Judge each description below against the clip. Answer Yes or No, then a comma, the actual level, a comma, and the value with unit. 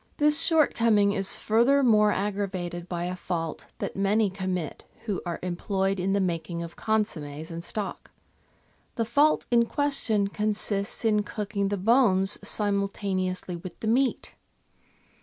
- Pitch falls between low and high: No, high, 200 Hz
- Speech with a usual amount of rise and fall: Yes, average, 3.2 semitones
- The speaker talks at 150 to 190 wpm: No, slow, 135 wpm